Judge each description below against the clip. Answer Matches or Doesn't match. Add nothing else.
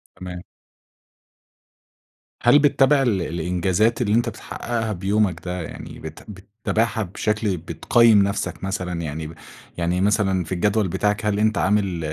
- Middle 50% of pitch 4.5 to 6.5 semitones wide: Doesn't match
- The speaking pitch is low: Matches